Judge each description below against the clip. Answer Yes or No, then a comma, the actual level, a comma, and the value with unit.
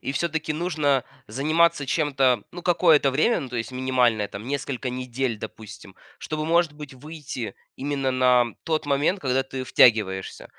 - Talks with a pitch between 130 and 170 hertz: Yes, low, 135 Hz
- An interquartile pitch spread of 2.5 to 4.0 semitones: Yes, average, 3.5 semitones